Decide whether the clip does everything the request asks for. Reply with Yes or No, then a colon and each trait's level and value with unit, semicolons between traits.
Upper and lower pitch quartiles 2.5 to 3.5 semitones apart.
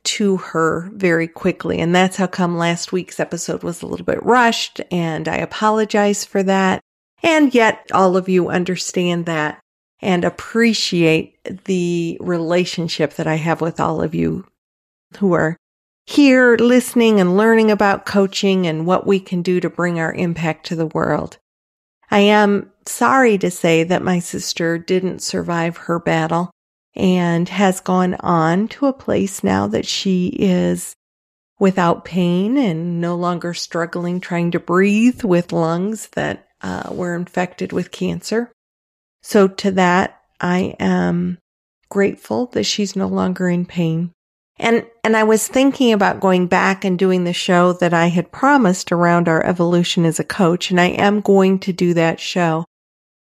Yes: average, 2.8 semitones